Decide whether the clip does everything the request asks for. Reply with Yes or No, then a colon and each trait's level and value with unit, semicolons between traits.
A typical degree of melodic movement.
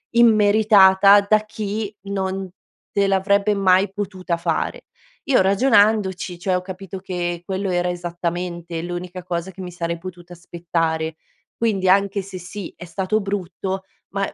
No: narrow, 2.3 semitones